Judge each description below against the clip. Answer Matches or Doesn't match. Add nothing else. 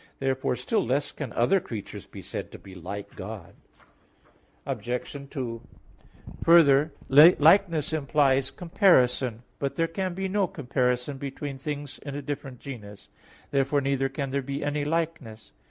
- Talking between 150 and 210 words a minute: Doesn't match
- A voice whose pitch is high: Doesn't match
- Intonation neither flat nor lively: Matches